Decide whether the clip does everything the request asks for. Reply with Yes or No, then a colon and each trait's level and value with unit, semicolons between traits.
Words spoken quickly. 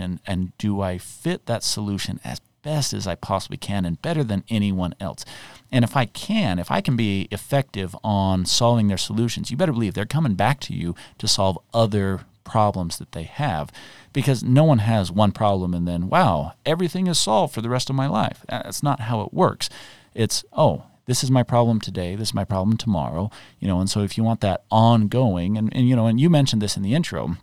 Yes: fast, 220 wpm